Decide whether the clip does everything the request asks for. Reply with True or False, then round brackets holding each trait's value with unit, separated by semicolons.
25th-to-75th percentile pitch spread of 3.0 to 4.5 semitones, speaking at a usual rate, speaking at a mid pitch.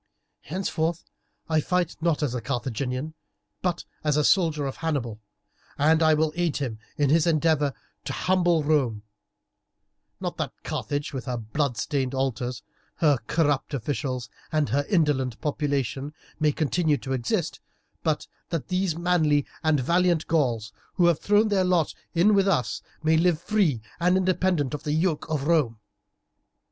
True (3.9 semitones; 150 wpm; 150 Hz)